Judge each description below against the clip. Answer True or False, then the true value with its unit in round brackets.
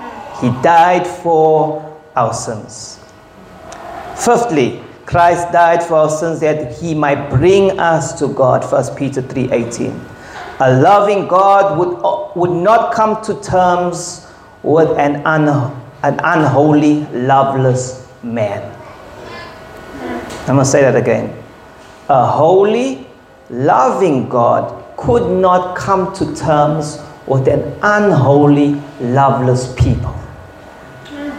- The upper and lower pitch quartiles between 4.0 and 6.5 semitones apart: True (4.6 semitones)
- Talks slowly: True (105 wpm)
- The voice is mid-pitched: True (155 Hz)